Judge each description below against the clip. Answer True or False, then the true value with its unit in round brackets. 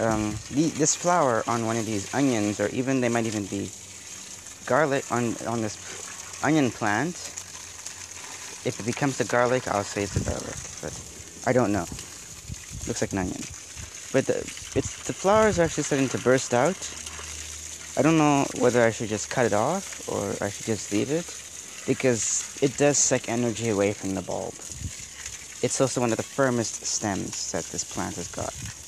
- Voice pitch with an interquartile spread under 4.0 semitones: False (5.1 semitones)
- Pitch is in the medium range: False (115 Hz)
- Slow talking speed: False (180 wpm)